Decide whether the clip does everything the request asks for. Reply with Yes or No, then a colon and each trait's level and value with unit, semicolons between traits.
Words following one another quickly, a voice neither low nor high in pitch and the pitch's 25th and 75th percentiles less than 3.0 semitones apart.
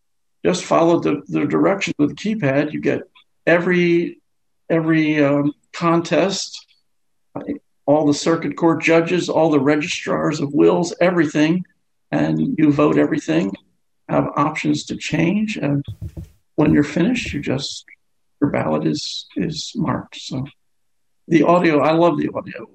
No: slow, 135 wpm; medium, 155 Hz; narrow, 2.6 semitones